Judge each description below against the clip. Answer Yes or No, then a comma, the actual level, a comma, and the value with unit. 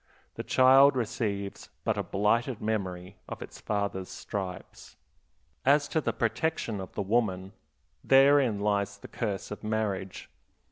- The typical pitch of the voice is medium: No, low, 105 Hz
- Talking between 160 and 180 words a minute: No, slow, 135 wpm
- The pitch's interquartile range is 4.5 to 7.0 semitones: No, average, 3.6 semitones